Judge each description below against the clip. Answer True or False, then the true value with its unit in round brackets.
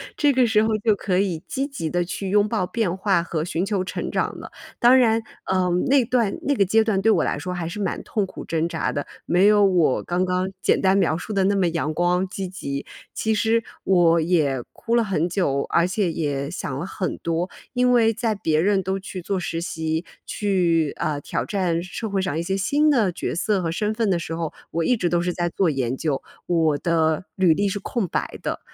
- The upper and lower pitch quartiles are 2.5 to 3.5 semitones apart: False (3.9 semitones)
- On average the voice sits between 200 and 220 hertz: False (185 Hz)